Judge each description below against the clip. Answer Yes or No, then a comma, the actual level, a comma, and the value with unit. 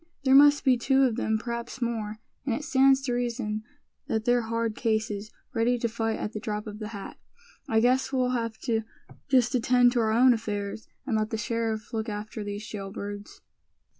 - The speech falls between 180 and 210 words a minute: Yes, average, 195 wpm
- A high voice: Yes, high, 230 Hz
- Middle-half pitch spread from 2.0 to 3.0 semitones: Yes, narrow, 2.4 semitones